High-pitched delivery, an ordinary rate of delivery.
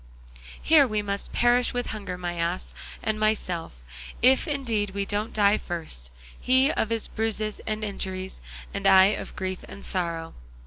Yes: high, 205 Hz; average, 160 wpm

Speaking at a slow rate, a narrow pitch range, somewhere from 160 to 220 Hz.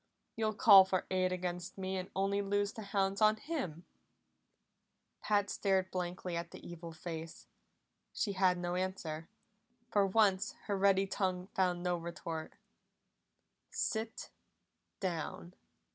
Yes: slow, 130 wpm; narrow, 2.2 semitones; medium, 185 Hz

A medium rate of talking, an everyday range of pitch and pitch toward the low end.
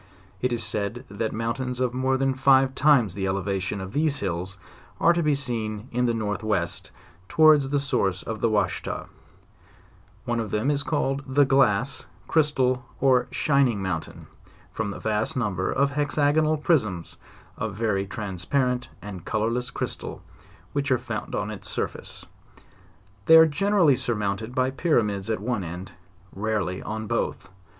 Yes: average, 155 wpm; average, 5.0 semitones; low, 120 Hz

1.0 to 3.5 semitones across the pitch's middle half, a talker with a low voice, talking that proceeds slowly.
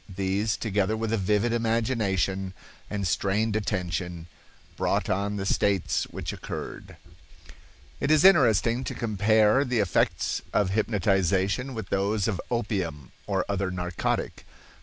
Yes: average, 2.9 semitones; low, 100 Hz; slow, 130 wpm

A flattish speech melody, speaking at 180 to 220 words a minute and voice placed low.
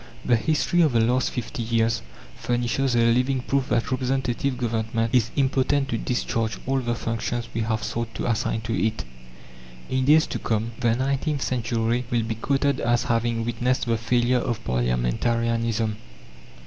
No: narrow, 2.1 semitones; average, 160 wpm; low, 120 Hz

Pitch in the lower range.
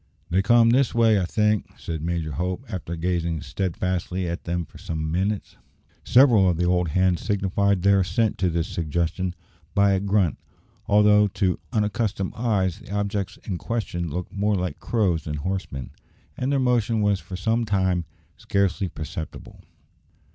Yes: very low, 95 Hz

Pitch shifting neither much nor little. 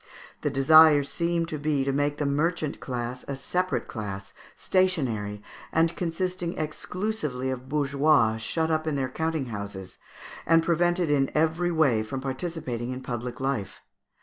Yes: average, 4.3 semitones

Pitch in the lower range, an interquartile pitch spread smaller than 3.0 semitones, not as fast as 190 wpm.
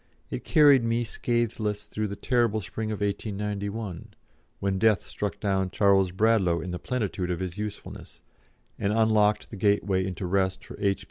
Yes: low, 105 Hz; narrow, 2.4 semitones; average, 160 wpm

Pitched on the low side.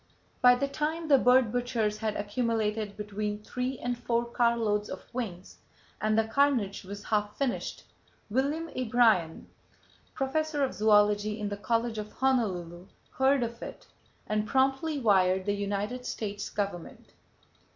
No: high, 220 Hz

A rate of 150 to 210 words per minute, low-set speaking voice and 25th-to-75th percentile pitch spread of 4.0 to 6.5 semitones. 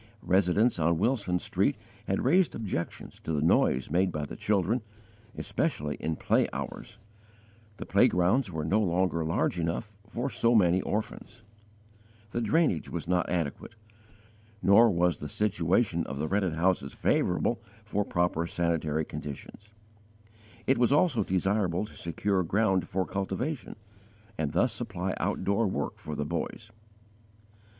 No: average, 140 wpm; very low, 95 Hz; average, 4.3 semitones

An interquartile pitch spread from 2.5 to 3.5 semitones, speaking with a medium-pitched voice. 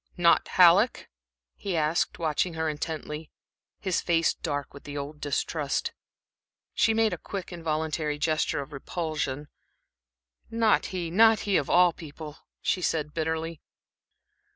Yes: average, 2.8 semitones; medium, 160 Hz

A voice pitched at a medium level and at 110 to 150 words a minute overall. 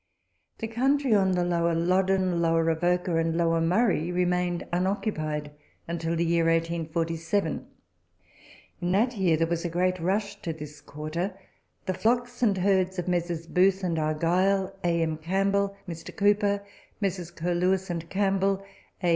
Yes: medium, 180 Hz; average, 145 wpm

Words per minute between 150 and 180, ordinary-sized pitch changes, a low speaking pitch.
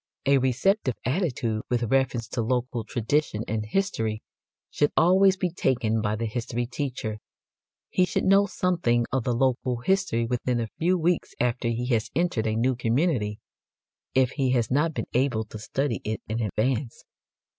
Yes: average, 165 wpm; average, 4.4 semitones; low, 125 Hz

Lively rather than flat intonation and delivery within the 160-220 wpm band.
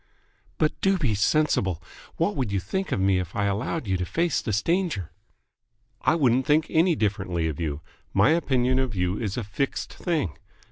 Yes: wide, 8.6 semitones; average, 190 wpm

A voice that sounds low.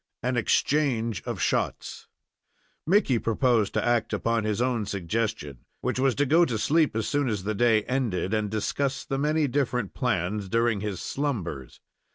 Yes: low, 115 Hz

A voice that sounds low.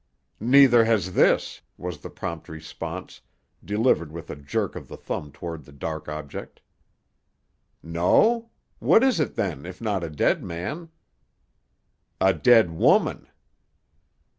Yes: very low, 90 Hz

